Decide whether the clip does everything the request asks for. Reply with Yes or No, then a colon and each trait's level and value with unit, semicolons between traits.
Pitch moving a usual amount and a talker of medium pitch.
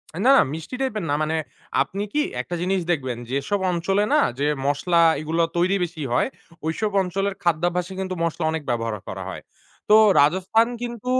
Yes: average, 3.8 semitones; medium, 175 Hz